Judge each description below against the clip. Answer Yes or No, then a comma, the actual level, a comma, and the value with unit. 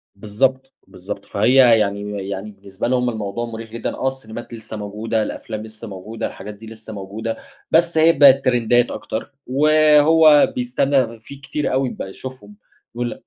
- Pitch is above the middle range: No, low, 115 Hz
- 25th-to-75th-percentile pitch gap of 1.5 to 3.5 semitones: No, average, 3.9 semitones